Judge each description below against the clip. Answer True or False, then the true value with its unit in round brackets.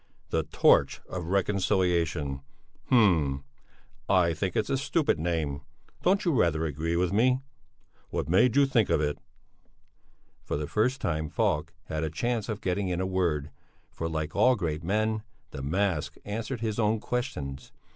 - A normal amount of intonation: False (5.8 semitones)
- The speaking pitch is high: False (90 Hz)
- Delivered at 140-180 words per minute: True (155 wpm)